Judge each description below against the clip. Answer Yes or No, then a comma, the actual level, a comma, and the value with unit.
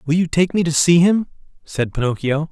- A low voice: No, medium, 160 Hz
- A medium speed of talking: No, fast, 215 wpm